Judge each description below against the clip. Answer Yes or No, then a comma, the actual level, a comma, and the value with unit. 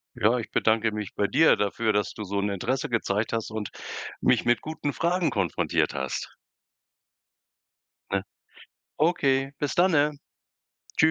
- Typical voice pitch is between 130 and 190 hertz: No, low, 115 Hz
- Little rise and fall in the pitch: No, wide, 5.7 semitones